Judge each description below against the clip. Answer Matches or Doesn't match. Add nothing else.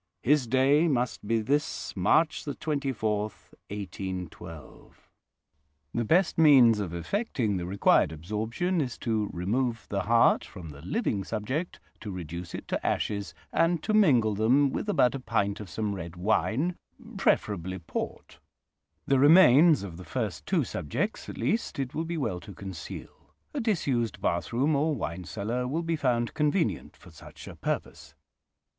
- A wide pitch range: Matches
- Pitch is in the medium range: Doesn't match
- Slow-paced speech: Doesn't match